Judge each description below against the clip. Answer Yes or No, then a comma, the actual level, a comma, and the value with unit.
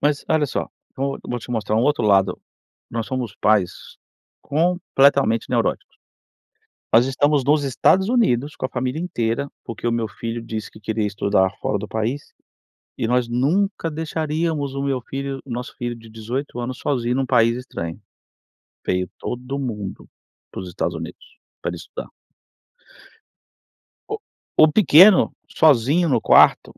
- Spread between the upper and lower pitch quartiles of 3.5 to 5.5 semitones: Yes, average, 4.3 semitones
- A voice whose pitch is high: No, low, 125 Hz